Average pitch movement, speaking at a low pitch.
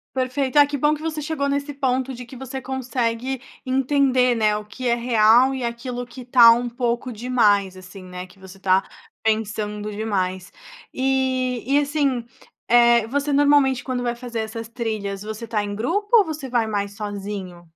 No: average, 3.8 semitones; high, 240 Hz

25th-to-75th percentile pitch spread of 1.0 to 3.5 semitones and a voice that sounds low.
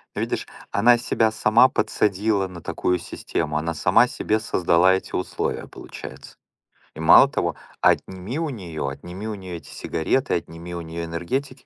No: average, 4.7 semitones; very low, 95 Hz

